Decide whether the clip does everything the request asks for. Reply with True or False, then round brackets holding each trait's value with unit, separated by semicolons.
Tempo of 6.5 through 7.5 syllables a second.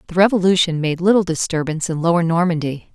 True (6.6 syllables/s)